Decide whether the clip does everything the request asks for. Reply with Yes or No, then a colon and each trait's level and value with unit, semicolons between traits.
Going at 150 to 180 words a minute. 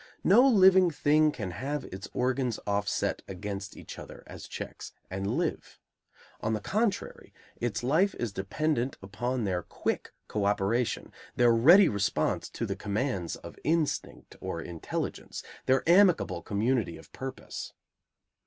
No: slow, 135 wpm